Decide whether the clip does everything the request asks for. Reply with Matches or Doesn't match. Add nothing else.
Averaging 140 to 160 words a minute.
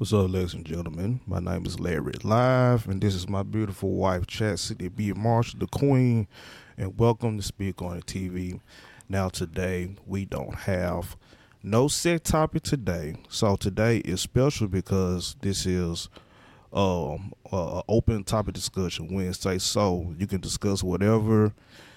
Matches